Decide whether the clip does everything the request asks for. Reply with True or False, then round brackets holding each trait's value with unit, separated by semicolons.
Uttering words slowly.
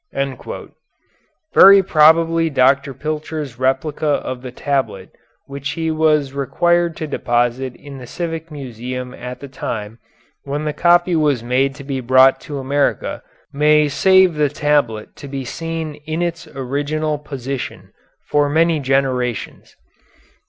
True (130 wpm)